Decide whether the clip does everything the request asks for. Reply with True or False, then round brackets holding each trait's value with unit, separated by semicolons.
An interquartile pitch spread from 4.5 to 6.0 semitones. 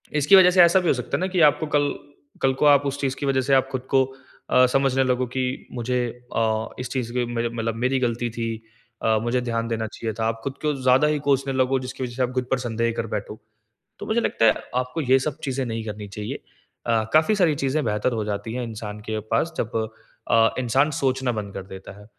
False (3.2 semitones)